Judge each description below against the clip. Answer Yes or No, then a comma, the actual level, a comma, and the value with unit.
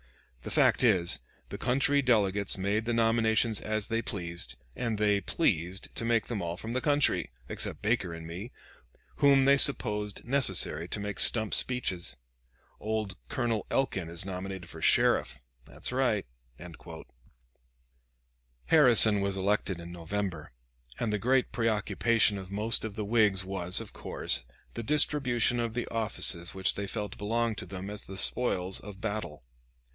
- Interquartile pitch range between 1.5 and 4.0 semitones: Yes, average, 3.5 semitones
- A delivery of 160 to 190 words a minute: No, average, 150 wpm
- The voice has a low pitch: Yes, low, 105 Hz